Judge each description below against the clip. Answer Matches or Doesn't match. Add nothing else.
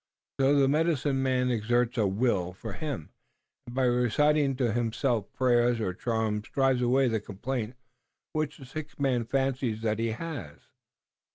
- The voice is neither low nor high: Doesn't match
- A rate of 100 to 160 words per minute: Matches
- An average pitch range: Matches